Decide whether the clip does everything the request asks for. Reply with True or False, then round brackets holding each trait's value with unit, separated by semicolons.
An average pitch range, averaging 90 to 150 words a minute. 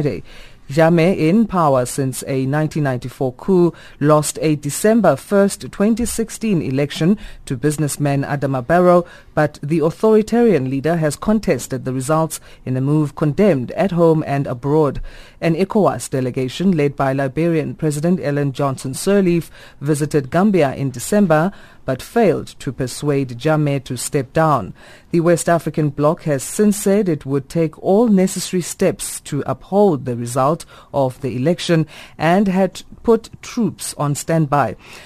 True (4.4 semitones; 140 wpm)